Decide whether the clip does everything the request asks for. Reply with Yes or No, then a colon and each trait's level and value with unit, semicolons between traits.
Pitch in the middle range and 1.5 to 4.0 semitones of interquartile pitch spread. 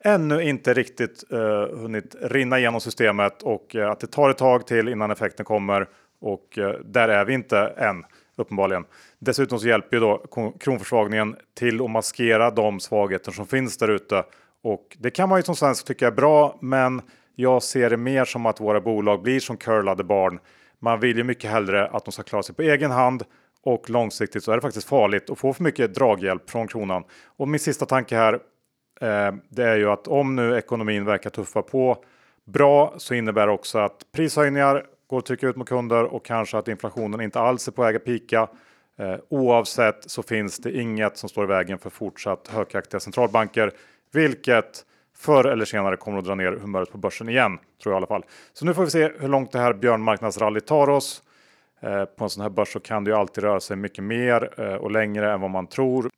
No: low, 115 Hz; average, 3.6 semitones